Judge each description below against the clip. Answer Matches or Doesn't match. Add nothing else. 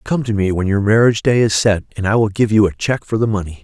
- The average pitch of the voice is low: Matches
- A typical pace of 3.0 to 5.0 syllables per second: Doesn't match